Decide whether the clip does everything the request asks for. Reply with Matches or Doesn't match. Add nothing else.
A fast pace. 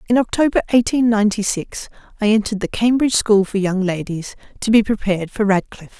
Doesn't match